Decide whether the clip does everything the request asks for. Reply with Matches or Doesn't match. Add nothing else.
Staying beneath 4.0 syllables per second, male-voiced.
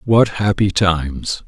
Matches